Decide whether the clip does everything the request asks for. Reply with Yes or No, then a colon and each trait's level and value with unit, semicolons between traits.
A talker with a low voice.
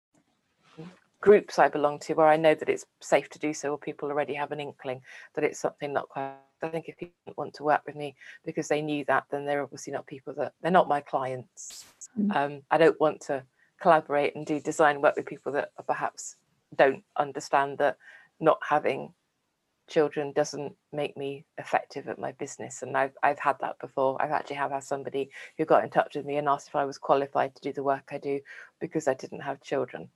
No: medium, 145 Hz